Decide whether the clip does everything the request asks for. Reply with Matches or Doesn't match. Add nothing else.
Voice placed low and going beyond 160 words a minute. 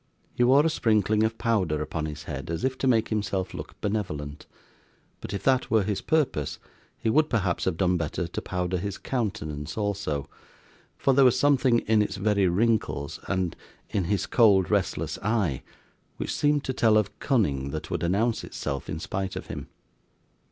Matches